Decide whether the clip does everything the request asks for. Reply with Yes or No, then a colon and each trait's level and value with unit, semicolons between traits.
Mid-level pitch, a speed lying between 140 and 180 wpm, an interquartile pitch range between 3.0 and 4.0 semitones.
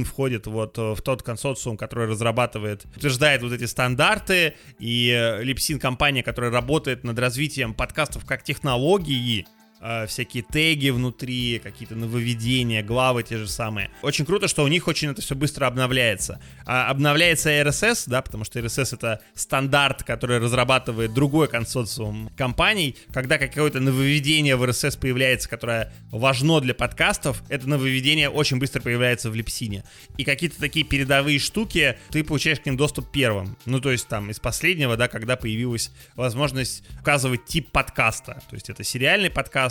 No: low, 130 Hz; average, 155 wpm; average, 3.7 semitones